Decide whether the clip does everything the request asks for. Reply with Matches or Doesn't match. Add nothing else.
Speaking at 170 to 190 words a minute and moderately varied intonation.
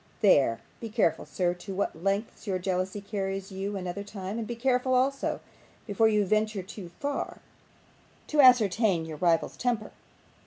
Doesn't match